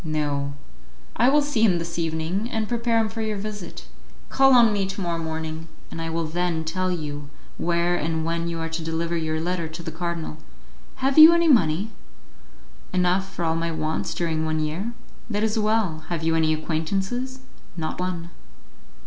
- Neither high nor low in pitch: Yes, medium, 170 Hz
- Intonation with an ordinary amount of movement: Yes, average, 4.6 semitones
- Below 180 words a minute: No, average, 185 wpm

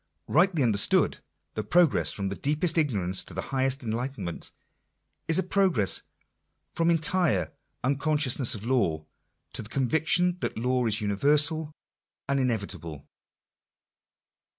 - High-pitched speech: No, low, 130 Hz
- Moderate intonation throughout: No, wide, 6.7 semitones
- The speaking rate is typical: No, slow, 120 wpm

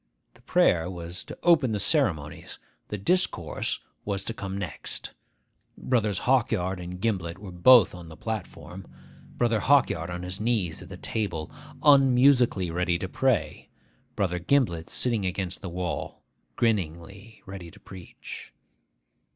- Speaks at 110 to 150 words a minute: Yes, slow, 135 wpm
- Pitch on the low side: Yes, very low, 95 Hz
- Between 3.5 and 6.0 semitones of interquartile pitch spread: Yes, average, 4.6 semitones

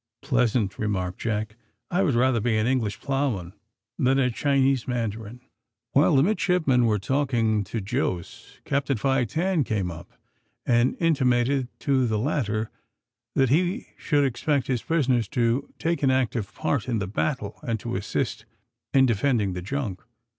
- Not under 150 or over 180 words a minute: Yes, average, 155 wpm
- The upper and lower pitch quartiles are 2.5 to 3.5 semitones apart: No, average, 4.2 semitones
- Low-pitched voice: Yes, low, 125 Hz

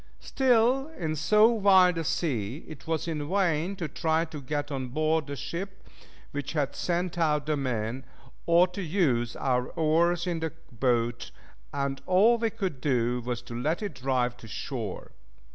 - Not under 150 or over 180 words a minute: Yes, average, 170 wpm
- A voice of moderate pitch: Yes, medium, 155 Hz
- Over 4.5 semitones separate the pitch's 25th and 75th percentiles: Yes, wide, 5.4 semitones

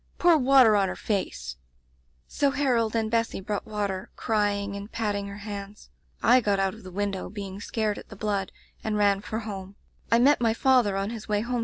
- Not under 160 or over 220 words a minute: Yes, average, 165 wpm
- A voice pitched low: No, high, 205 Hz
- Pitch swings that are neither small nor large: No, narrow, 2.0 semitones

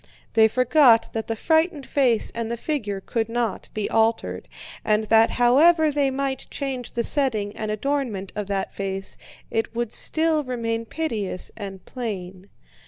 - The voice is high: Yes, high, 230 Hz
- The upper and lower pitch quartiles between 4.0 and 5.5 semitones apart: Yes, average, 4.3 semitones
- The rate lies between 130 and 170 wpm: Yes, average, 155 wpm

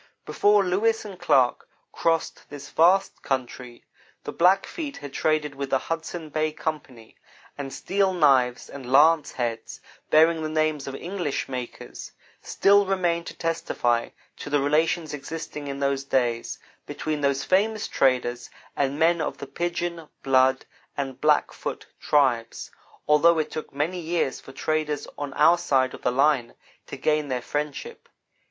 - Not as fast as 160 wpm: Yes, average, 150 wpm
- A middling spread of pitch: Yes, average, 3.7 semitones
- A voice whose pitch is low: No, medium, 150 Hz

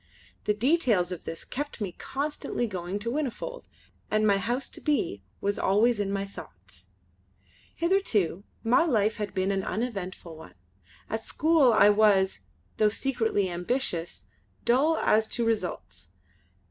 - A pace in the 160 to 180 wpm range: No, average, 140 wpm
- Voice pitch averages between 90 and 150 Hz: No, high, 215 Hz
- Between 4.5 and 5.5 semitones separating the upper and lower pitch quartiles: Yes, average, 4.8 semitones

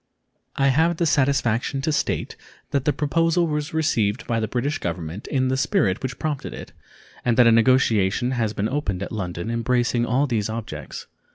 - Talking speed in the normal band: Yes, average, 180 wpm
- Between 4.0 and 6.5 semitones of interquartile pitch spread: Yes, average, 4.6 semitones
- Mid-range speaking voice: No, low, 125 Hz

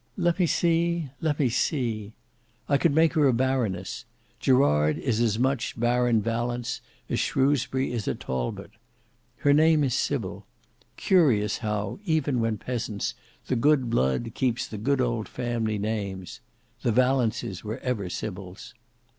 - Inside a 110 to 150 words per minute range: Yes, average, 140 wpm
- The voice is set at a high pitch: No, low, 120 Hz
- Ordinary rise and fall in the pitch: Yes, average, 4.4 semitones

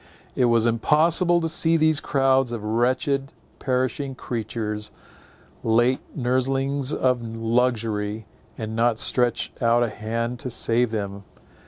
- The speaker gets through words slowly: Yes, slow, 125 wpm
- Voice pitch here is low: Yes, low, 120 Hz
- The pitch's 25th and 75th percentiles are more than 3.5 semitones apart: No, average, 2.9 semitones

